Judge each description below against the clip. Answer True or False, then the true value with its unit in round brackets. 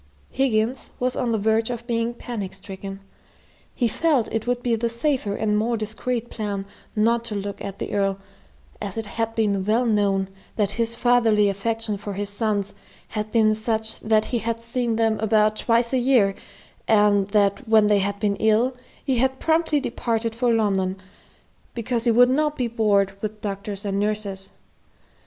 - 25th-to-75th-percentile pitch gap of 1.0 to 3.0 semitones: True (2.6 semitones)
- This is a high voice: True (220 Hz)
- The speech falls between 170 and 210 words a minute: True (175 wpm)